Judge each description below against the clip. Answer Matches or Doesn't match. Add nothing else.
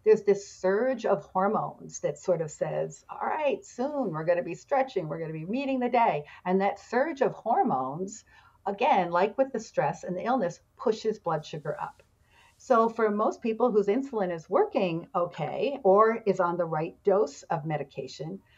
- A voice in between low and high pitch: Doesn't match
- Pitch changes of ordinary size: Doesn't match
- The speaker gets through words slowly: Doesn't match